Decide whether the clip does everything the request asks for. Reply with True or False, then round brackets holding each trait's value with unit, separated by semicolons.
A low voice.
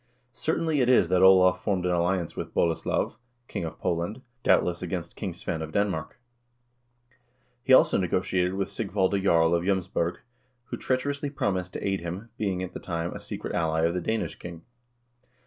True (90 Hz)